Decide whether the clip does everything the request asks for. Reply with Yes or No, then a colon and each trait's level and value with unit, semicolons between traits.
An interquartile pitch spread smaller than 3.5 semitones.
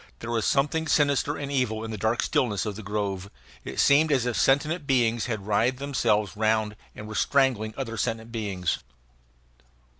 No: average, 4.1 semitones